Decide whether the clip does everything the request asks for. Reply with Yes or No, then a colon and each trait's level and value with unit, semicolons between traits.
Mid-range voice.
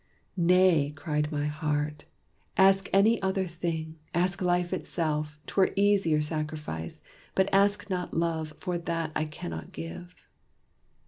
Yes: medium, 165 Hz